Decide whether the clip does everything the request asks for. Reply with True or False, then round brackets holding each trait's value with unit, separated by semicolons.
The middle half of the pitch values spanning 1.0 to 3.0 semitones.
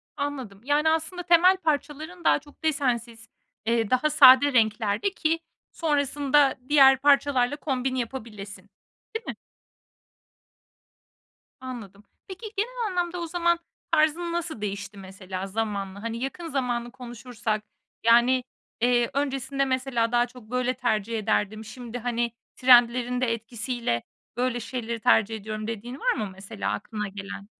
False (4.5 semitones)